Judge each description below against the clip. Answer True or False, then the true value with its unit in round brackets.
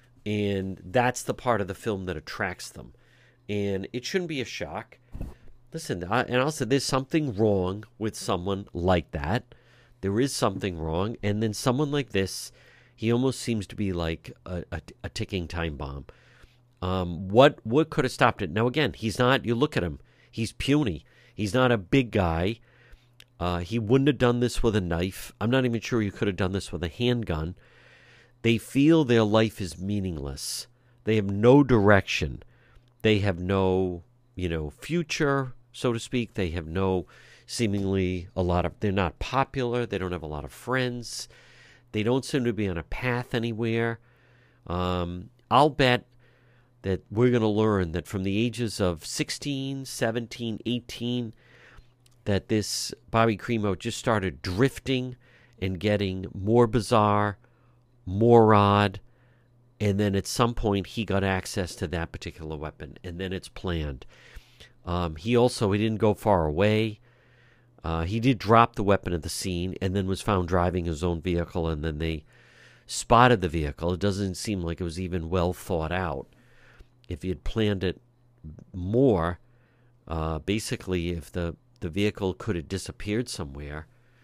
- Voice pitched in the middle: False (110 Hz)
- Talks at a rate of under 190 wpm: True (170 wpm)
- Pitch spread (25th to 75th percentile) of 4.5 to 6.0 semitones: True (4.8 semitones)